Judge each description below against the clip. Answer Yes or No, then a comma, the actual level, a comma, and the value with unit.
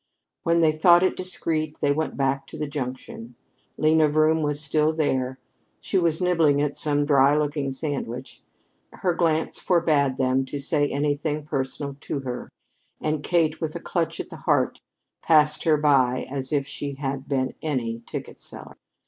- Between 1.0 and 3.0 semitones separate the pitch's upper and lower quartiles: Yes, narrow, 2.4 semitones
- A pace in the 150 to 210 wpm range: Yes, average, 165 wpm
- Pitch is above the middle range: No, medium, 150 Hz